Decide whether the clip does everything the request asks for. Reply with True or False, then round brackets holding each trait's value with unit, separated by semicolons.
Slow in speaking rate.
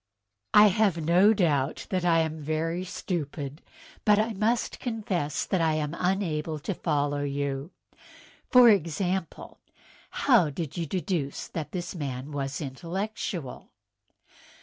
True (130 wpm)